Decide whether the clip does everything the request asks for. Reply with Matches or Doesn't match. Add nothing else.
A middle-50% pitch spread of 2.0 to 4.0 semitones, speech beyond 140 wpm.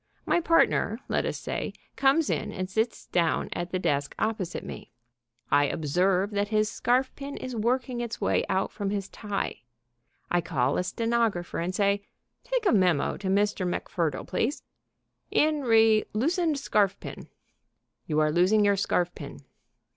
Doesn't match